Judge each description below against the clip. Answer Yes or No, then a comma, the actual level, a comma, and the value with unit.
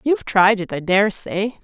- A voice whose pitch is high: Yes, high, 200 Hz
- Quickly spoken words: Yes, fast, 220 wpm